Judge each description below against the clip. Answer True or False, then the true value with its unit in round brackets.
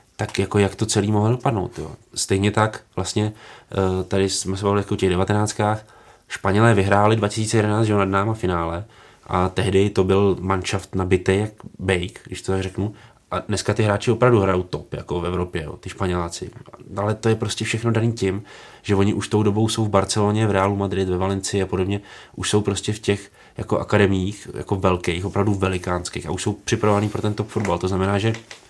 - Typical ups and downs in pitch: False (2.0 semitones)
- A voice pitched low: True (100 Hz)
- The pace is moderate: False (200 wpm)